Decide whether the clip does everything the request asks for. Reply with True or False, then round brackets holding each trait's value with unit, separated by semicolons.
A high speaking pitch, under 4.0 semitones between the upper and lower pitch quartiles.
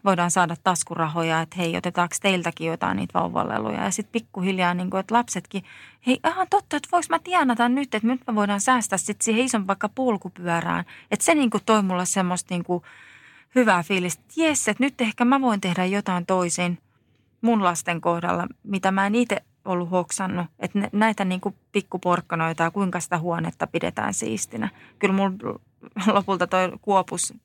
False (195 Hz; 4.3 semitones)